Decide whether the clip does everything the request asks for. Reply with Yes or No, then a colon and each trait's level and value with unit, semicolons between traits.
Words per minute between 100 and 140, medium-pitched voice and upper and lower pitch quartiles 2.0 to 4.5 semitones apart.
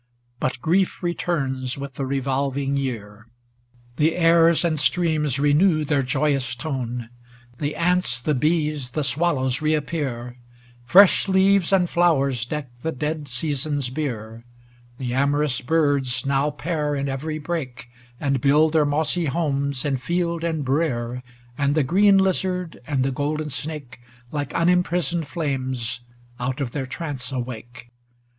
Yes: slow, 135 wpm; medium, 145 Hz; average, 3.8 semitones